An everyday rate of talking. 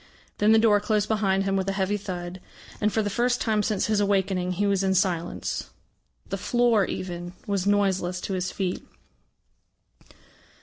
Yes: average, 170 wpm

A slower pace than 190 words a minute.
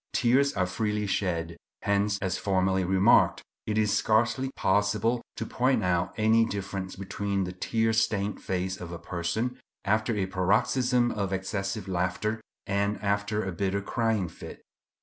Yes: average, 150 wpm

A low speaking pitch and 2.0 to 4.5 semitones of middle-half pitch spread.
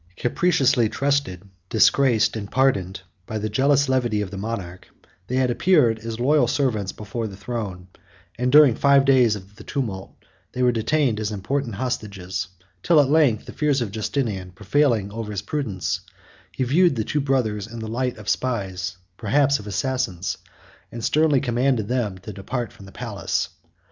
No: low, 115 Hz; average, 4.9 semitones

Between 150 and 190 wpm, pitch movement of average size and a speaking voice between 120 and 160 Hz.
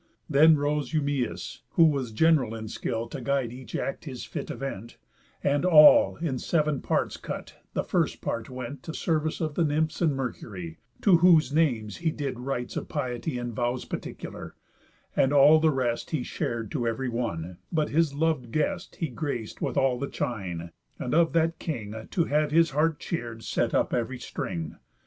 Yes: average, 180 wpm; average, 4.7 semitones; low, 135 Hz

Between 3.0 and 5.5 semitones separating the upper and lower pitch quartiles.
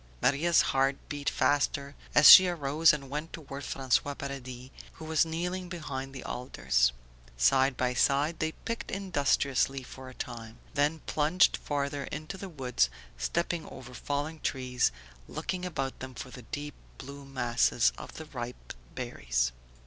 Yes: average, 3.4 semitones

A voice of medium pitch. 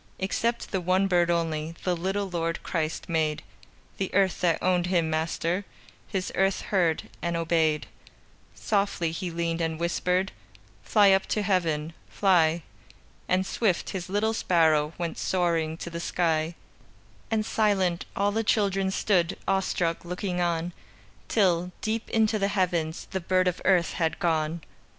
Yes: medium, 175 Hz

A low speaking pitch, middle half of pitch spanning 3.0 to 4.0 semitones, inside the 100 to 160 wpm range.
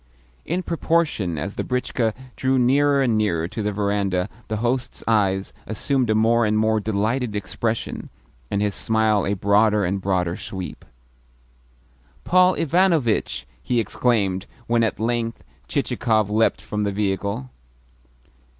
Yes: low, 110 Hz; average, 3.3 semitones; slow, 135 wpm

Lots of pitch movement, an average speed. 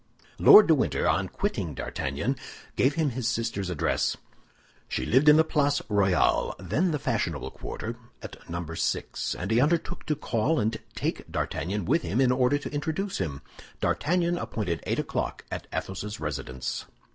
Yes: wide, 8.6 semitones; average, 155 wpm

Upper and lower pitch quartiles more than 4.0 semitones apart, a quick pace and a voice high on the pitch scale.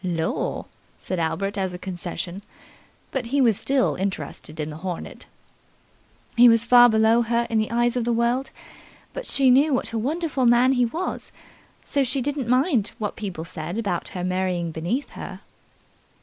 No: wide, 5.6 semitones; average, 170 wpm; high, 230 Hz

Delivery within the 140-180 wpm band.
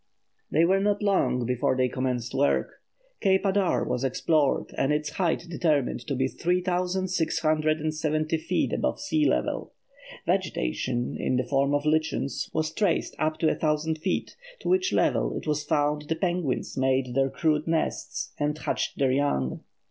Yes: average, 160 wpm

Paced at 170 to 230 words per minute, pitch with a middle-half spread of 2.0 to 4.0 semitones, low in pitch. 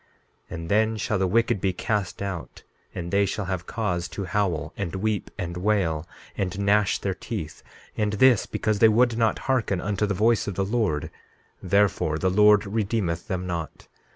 Yes: average, 180 wpm; average, 2.9 semitones; low, 100 Hz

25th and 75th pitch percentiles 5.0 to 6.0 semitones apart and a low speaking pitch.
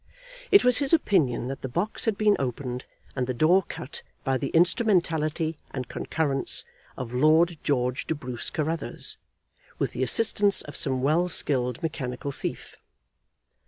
No: average, 5.3 semitones; medium, 150 Hz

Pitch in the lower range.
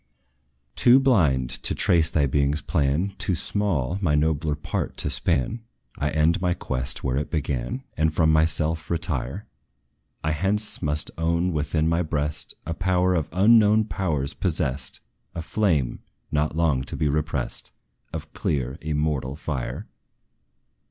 Yes: very low, 80 Hz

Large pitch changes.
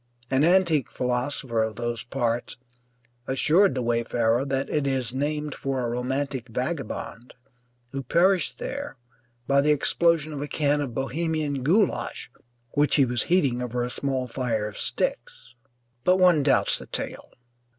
No: average, 3.6 semitones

